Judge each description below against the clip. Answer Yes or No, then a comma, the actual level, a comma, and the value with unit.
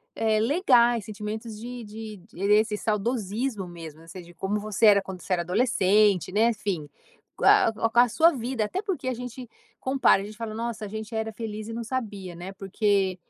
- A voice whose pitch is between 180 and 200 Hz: No, high, 215 Hz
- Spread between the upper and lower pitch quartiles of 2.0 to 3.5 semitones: Yes, average, 3.1 semitones